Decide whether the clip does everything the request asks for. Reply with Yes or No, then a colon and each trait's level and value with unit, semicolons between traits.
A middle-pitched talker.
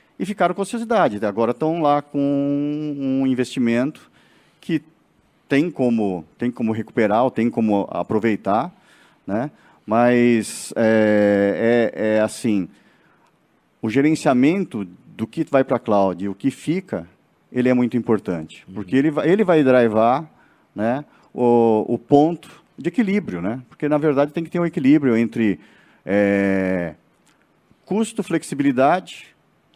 No: low, 125 Hz